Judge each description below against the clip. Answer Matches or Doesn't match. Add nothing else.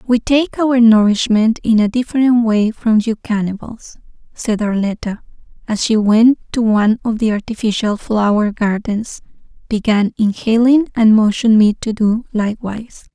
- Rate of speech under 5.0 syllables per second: Matches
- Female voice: Matches